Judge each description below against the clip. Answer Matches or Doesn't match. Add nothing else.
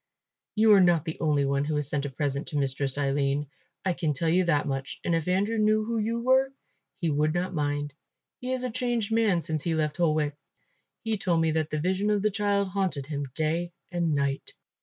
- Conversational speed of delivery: Doesn't match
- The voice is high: Doesn't match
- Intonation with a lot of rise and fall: Matches